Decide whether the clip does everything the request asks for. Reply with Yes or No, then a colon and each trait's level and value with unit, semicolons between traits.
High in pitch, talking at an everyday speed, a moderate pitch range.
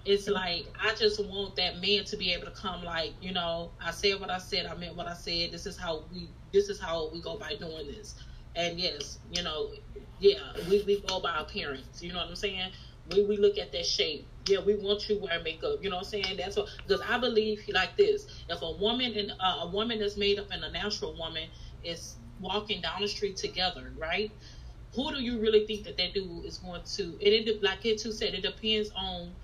No: high, 200 Hz; fast, 235 wpm; average, 3.4 semitones